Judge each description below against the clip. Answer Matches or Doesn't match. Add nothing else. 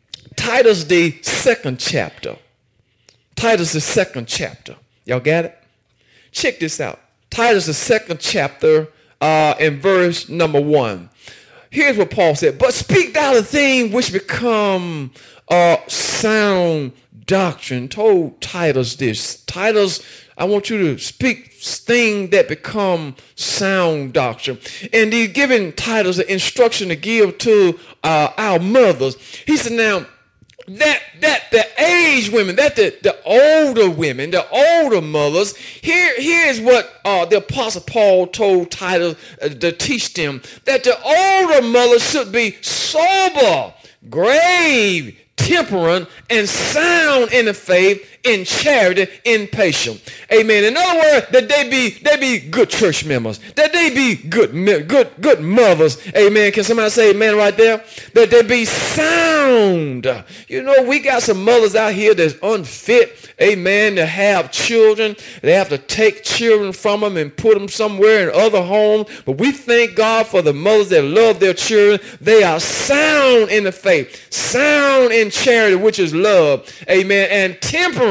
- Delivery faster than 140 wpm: Matches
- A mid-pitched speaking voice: Doesn't match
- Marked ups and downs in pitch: Matches